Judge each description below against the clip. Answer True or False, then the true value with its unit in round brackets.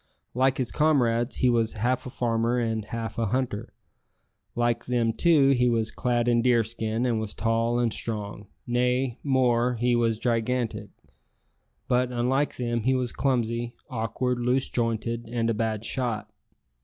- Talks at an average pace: True (155 wpm)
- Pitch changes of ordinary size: False (1.6 semitones)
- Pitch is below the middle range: True (120 Hz)